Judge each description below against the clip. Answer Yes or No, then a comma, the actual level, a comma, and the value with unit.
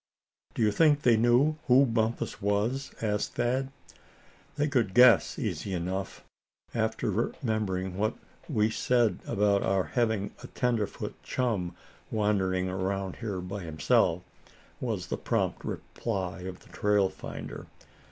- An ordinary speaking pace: No, slow, 130 wpm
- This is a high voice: No, low, 105 Hz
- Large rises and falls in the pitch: No, average, 3.9 semitones